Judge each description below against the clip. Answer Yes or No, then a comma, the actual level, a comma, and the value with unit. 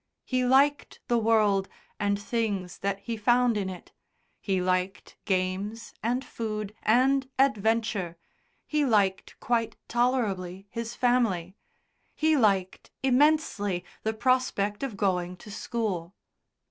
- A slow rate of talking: Yes, slow, 120 wpm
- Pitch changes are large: No, average, 4.2 semitones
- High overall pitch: Yes, high, 215 Hz